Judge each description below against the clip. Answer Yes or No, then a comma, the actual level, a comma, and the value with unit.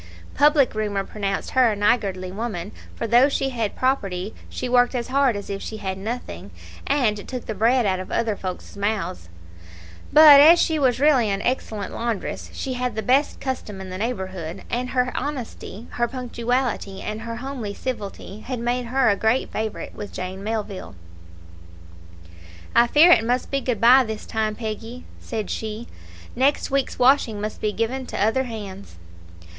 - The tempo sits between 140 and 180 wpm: Yes, average, 170 wpm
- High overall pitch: Yes, high, 230 Hz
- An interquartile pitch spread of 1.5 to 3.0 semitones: No, average, 3.8 semitones